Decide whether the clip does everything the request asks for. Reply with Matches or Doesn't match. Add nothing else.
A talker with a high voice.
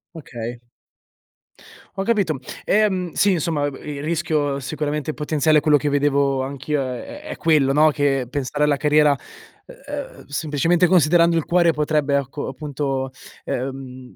Doesn't match